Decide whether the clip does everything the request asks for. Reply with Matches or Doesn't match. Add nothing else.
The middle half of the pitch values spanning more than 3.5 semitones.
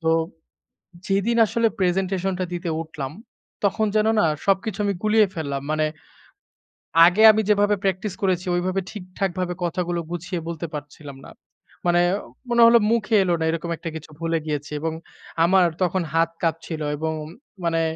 Doesn't match